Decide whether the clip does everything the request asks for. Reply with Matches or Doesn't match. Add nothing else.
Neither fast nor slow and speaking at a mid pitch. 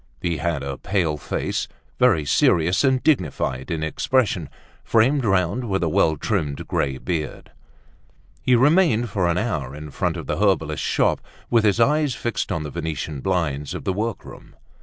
Doesn't match